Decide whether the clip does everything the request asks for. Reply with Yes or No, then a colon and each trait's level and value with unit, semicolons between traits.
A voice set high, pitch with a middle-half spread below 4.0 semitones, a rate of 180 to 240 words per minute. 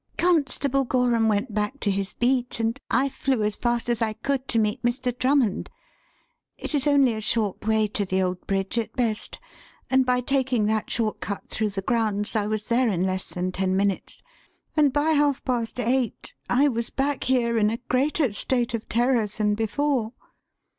Yes: high, 235 Hz; average, 3.6 semitones; average, 190 wpm